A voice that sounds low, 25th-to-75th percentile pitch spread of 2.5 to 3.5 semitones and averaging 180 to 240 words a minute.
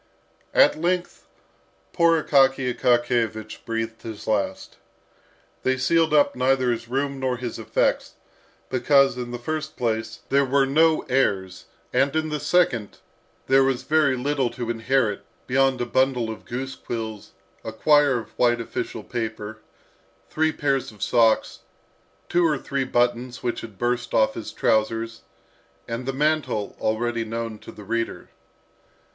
No: low, 125 Hz; average, 3.2 semitones; average, 145 wpm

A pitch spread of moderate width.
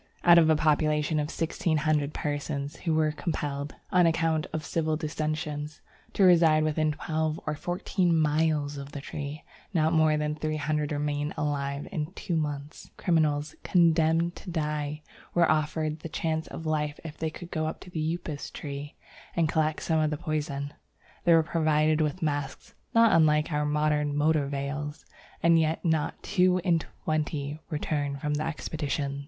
No: narrow, 1.5 semitones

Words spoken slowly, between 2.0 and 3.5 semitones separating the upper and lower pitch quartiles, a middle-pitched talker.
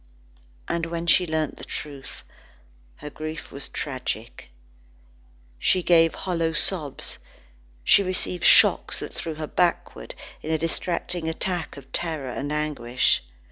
Yes: slow, 130 wpm; average, 2.9 semitones; medium, 160 Hz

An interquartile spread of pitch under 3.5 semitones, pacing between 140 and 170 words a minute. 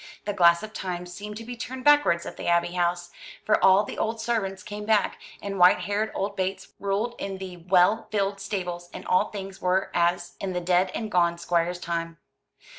No: average, 2.9 semitones; average, 200 wpm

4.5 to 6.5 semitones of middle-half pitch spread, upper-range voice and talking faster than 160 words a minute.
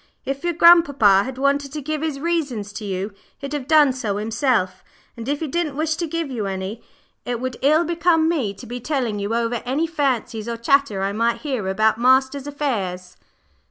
Yes: wide, 5.4 semitones; very high, 260 Hz; average, 195 wpm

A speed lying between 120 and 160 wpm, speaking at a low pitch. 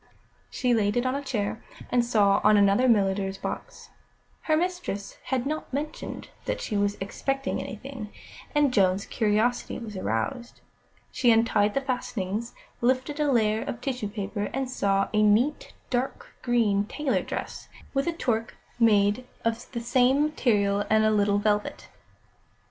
No: average, 155 wpm; high, 225 Hz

